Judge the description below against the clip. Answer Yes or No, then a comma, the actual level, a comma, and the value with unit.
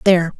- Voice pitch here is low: No, medium, 175 Hz